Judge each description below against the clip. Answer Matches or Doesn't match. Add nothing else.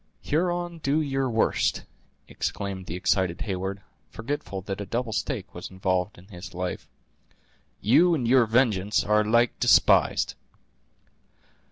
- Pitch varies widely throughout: Matches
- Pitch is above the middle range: Doesn't match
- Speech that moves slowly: Matches